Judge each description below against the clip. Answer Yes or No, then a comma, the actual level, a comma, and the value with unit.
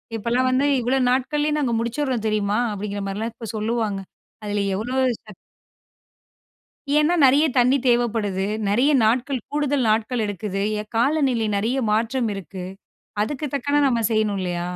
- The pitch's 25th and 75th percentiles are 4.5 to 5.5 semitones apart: No, average, 3.9 semitones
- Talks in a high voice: Yes, high, 230 Hz